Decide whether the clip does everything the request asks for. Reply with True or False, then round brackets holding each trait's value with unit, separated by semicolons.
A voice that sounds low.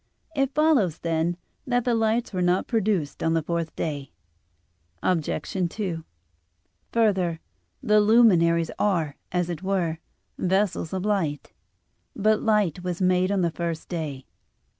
False (180 Hz)